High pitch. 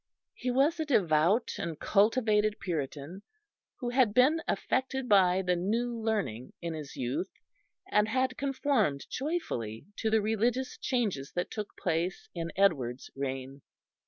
Yes: high, 205 Hz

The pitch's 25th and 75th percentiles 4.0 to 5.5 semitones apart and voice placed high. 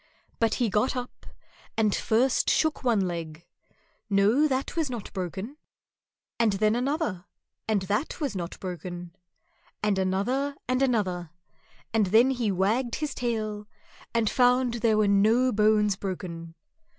Yes: average, 4.5 semitones; high, 215 Hz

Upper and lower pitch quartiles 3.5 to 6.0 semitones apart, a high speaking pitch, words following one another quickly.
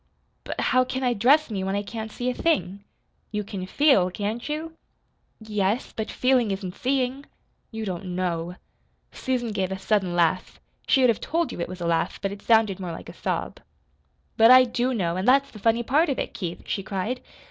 Yes: average, 5.1 semitones; high, 215 Hz; fast, 210 wpm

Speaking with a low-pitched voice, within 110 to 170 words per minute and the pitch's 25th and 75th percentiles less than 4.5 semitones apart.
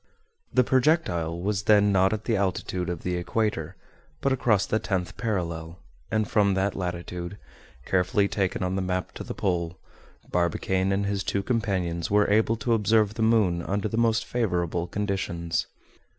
Yes: very low, 95 Hz; average, 165 wpm; average, 3.5 semitones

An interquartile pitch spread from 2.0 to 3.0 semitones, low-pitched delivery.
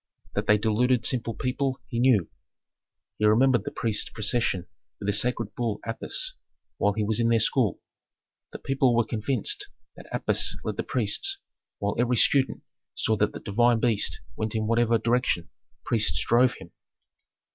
Yes: average, 2.7 semitones; low, 115 Hz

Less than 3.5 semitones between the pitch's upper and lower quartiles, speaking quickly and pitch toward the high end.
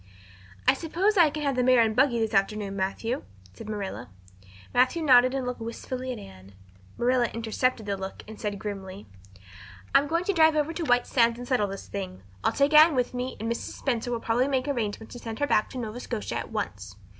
No: average, 4.0 semitones; fast, 215 wpm; high, 245 Hz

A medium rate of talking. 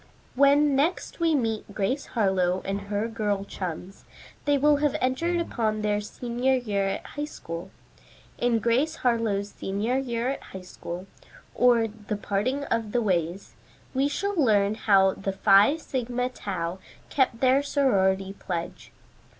Yes: average, 145 wpm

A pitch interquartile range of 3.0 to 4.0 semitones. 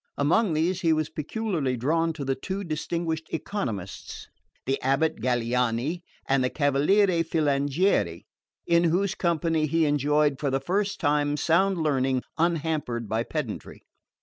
Yes: average, 3.7 semitones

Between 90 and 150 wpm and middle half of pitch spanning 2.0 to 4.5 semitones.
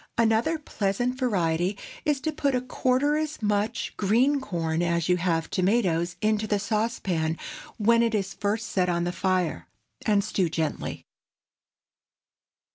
No: average, 140 wpm; average, 5.1 semitones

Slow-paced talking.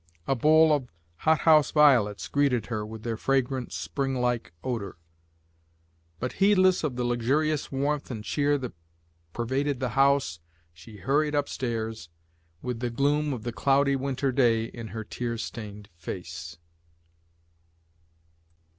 Yes: slow, 130 wpm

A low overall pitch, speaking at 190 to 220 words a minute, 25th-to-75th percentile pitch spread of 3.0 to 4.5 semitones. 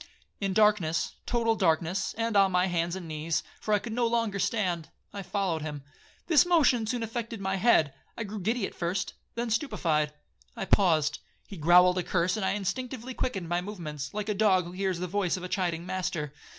No: high, 190 Hz; average, 195 wpm; average, 4.2 semitones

